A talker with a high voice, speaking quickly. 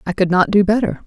Yes: high, 200 Hz; fast, 280 wpm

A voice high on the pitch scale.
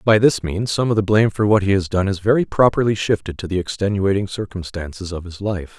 No: low, 100 Hz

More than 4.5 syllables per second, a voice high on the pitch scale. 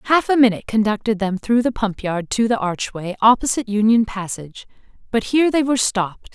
Yes: 6.0 syllables/s; high, 220 Hz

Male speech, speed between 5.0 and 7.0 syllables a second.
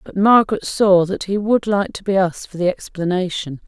No: female; 5.4 syllables/s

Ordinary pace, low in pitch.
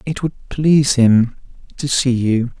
Yes: average, 160 wpm; low, 130 Hz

